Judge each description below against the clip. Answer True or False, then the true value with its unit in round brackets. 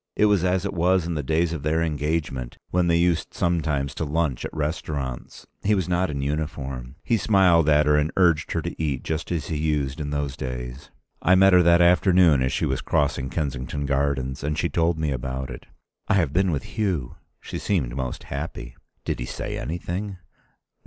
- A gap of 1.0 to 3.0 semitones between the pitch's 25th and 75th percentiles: False (4.0 semitones)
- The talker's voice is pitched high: False (75 Hz)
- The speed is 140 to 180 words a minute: False (200 wpm)